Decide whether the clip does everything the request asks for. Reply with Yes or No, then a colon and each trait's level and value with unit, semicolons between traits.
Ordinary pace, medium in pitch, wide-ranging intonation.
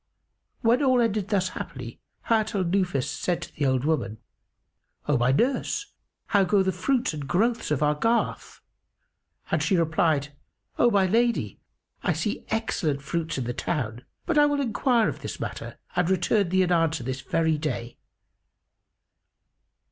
Yes: average, 160 wpm; medium, 180 Hz; wide, 7.0 semitones